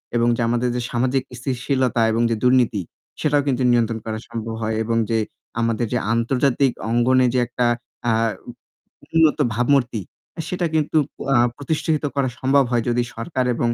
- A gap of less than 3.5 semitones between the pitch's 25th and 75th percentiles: Yes, average, 2.8 semitones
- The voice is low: Yes, low, 125 Hz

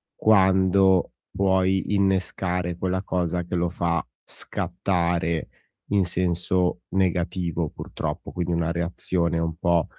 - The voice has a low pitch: Yes, very low, 90 Hz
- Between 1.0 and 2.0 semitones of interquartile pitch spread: Yes, narrow, 1.6 semitones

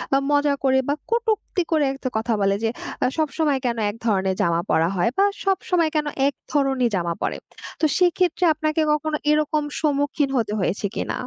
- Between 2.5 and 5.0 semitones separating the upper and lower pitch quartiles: No, wide, 5.5 semitones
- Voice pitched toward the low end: No, very high, 285 Hz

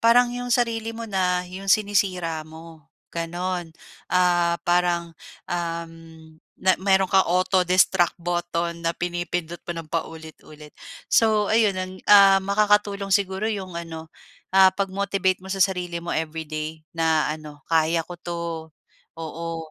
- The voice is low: No, medium, 175 Hz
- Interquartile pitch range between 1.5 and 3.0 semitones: Yes, average, 2.7 semitones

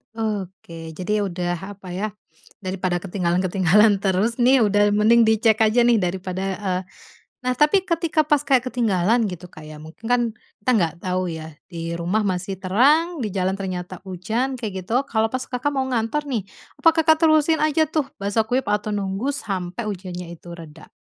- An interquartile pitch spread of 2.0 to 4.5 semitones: No, wide, 5.4 semitones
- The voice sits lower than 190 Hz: No, high, 205 Hz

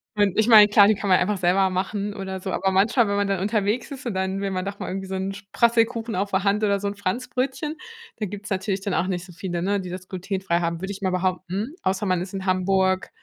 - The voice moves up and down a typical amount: No, narrow, 1.7 semitones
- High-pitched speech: Yes, high, 195 Hz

